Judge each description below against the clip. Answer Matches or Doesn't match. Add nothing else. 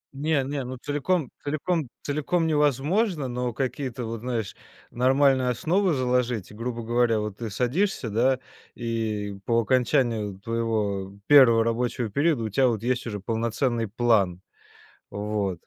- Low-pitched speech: Matches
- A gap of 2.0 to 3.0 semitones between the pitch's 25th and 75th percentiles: Doesn't match